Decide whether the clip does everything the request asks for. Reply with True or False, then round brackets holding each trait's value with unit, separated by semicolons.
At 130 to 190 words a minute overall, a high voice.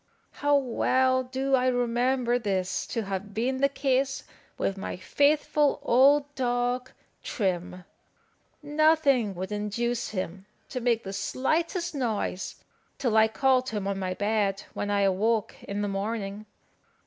True (135 wpm; 235 Hz)